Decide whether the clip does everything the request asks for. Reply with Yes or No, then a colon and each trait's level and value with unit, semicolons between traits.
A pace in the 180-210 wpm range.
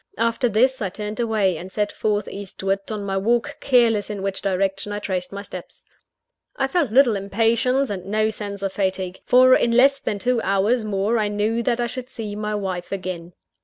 Yes: average, 200 wpm